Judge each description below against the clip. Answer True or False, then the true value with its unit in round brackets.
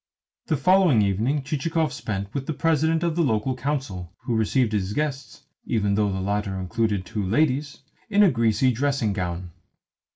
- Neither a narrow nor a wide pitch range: False (6.5 semitones)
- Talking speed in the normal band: True (165 wpm)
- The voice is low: True (115 Hz)